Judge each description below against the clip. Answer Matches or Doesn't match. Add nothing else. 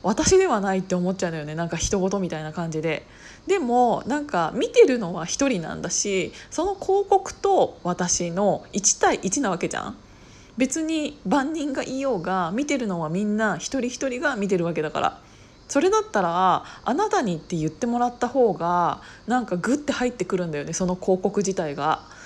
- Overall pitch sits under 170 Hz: Doesn't match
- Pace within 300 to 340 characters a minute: Doesn't match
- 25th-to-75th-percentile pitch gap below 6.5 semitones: Doesn't match